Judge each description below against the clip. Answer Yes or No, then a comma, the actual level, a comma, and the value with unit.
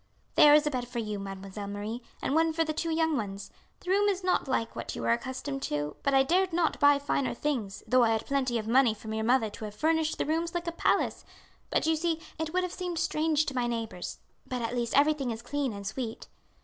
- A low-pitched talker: No, very high, 270 Hz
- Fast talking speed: Yes, fast, 245 wpm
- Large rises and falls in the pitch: Yes, wide, 6.0 semitones